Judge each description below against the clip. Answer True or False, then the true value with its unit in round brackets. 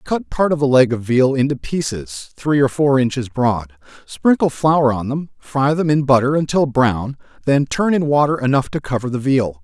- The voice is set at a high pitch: False (135 Hz)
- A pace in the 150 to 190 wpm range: False (200 wpm)